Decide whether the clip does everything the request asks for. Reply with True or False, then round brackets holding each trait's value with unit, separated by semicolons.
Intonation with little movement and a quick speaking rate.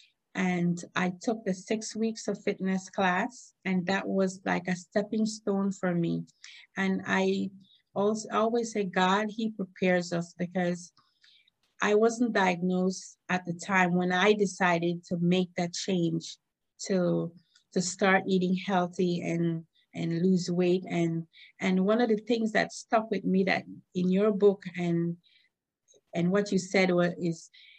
False (2.3 semitones; 155 wpm)